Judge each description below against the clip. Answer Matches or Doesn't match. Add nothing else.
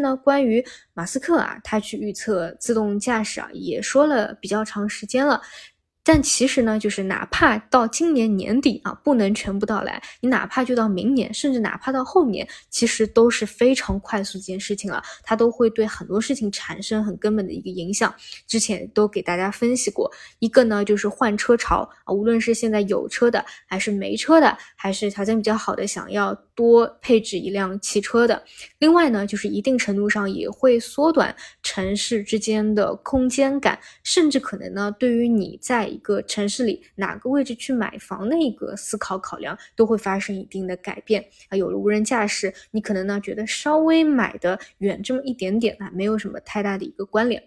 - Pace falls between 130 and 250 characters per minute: Doesn't match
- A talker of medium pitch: Doesn't match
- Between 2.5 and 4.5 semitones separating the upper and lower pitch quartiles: Matches